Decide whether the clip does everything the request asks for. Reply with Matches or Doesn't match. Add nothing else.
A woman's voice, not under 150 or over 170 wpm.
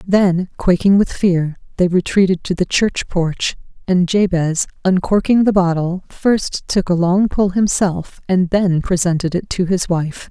Matches